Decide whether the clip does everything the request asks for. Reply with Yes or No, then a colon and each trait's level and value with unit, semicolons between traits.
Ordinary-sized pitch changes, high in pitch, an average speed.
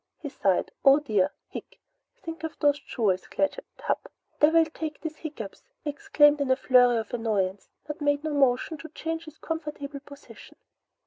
Yes: average, 4.1 semitones; very high, 290 Hz; average, 170 wpm